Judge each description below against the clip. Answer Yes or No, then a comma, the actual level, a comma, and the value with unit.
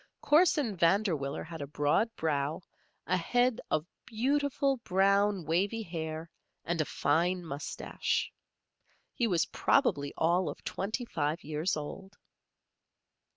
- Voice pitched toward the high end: No, medium, 180 Hz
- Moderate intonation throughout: No, wide, 5.7 semitones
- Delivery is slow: Yes, slow, 115 wpm